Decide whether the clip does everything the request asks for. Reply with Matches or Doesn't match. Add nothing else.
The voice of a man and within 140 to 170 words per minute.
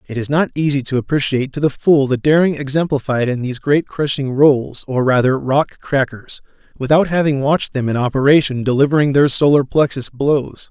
Doesn't match